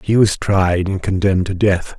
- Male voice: Yes, male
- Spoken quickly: Yes, fast, 210 wpm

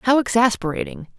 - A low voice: No, high, 225 Hz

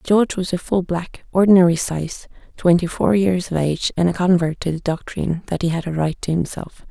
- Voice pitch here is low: No, medium, 175 Hz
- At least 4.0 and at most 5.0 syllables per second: No, 5.6 syllables/s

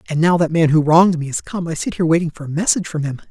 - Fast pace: Yes, fast, 325 wpm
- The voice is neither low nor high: Yes, medium, 160 Hz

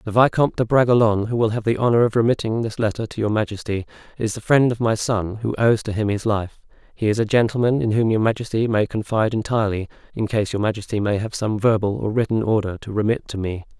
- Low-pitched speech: Yes, low, 110 Hz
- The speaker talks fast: Yes, fast, 235 wpm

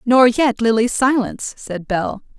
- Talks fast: No, average, 150 wpm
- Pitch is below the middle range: No, high, 235 Hz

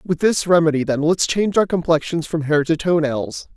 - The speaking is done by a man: Yes, male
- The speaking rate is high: Yes, fast, 220 wpm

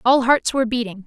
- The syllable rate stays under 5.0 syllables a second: No, 6.2 syllables/s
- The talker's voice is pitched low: No, high, 240 Hz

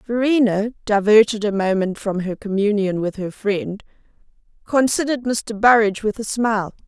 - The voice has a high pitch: Yes, high, 210 Hz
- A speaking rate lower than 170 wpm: Yes, average, 140 wpm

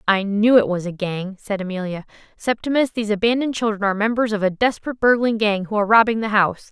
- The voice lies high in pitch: Yes, high, 210 Hz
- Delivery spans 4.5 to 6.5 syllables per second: No, 6.7 syllables/s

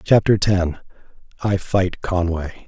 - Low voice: Yes, very low, 95 Hz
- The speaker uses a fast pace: No, slow, 90 wpm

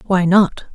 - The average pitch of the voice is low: No, medium, 185 Hz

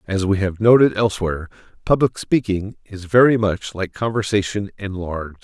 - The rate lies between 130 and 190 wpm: Yes, average, 145 wpm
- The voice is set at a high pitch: No, low, 100 Hz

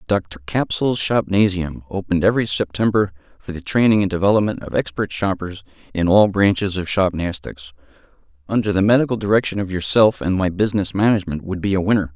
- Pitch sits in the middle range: No, very low, 95 Hz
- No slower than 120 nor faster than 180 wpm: Yes, average, 165 wpm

